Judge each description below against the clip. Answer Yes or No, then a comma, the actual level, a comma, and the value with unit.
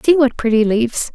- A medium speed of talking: No, fast, 210 wpm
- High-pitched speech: Yes, high, 245 Hz